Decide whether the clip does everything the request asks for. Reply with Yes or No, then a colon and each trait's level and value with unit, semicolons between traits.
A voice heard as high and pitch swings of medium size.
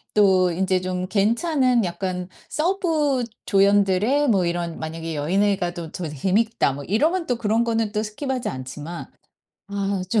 Yes: high, 200 Hz; average, 4.8 semitones